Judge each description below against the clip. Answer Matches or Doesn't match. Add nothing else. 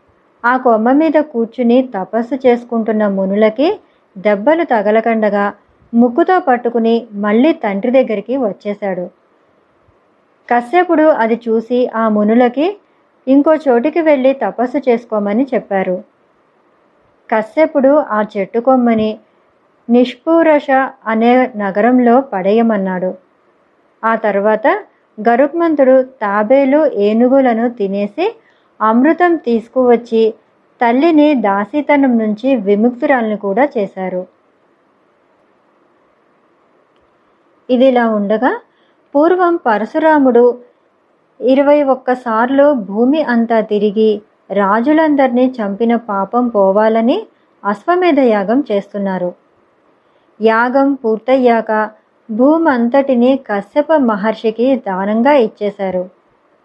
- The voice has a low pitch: Doesn't match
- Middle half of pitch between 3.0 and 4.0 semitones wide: Doesn't match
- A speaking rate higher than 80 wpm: Doesn't match